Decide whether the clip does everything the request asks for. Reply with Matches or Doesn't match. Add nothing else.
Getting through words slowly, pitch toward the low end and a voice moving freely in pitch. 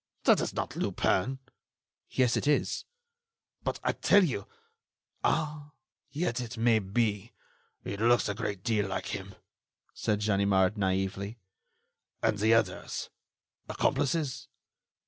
Doesn't match